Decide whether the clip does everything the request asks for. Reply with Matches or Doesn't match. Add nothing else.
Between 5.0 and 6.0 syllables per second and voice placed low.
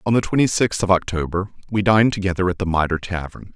Doesn't match